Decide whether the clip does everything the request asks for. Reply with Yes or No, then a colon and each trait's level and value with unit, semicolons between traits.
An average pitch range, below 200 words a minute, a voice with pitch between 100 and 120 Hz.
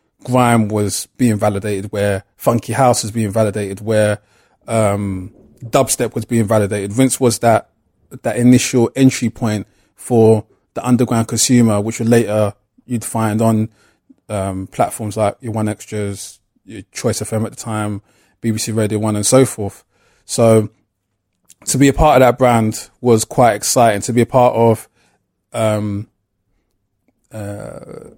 No: narrow, 2.3 semitones; average, 145 wpm; low, 110 Hz